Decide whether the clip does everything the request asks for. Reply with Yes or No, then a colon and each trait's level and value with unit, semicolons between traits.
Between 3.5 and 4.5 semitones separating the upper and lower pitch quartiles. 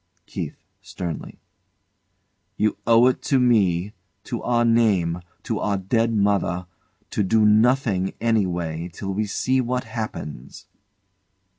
Yes: average, 4.2 semitones